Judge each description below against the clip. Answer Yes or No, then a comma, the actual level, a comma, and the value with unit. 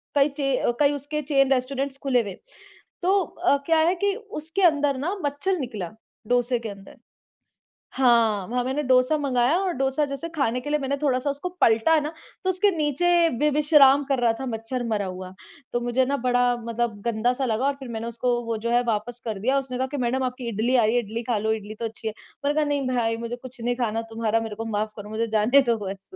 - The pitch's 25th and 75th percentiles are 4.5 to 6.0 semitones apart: No, average, 3.8 semitones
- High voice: Yes, very high, 250 Hz